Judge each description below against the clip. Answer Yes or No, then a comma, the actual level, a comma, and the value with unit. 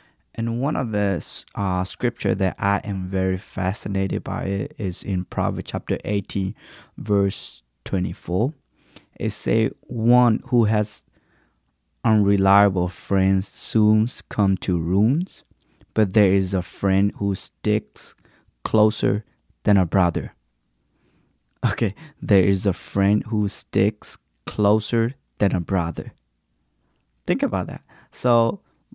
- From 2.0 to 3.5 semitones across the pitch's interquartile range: Yes, narrow, 2.5 semitones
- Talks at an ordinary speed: No, slow, 120 wpm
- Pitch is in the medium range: No, low, 100 Hz